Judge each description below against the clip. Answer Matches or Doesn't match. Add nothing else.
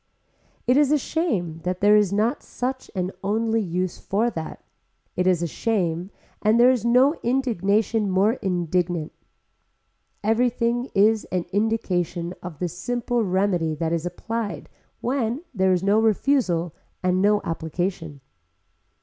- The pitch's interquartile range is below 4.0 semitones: Doesn't match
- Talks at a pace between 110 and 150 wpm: Matches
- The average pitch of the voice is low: Doesn't match